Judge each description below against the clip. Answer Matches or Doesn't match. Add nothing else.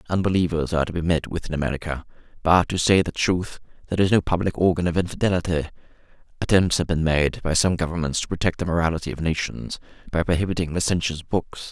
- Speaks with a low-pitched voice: Matches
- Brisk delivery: Doesn't match